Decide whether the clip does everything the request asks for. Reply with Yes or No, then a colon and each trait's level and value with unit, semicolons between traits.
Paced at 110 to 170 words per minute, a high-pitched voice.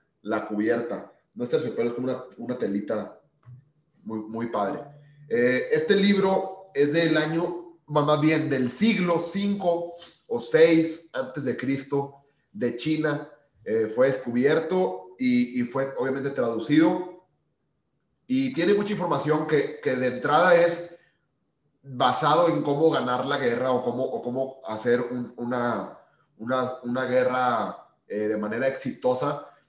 No: average, 135 wpm; medium, 140 Hz